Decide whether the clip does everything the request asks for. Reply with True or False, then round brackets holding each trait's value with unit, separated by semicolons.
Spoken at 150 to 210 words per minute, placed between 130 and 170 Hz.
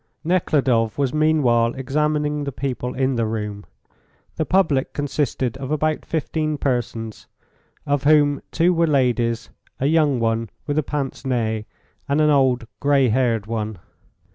False (140 wpm; 135 Hz)